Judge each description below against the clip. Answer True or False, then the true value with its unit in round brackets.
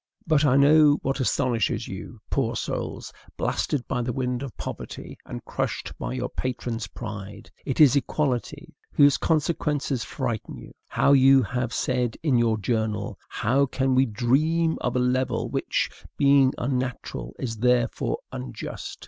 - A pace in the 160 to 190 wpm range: False (150 wpm)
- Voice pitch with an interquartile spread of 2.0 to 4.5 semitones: True (2.8 semitones)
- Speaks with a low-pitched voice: True (130 Hz)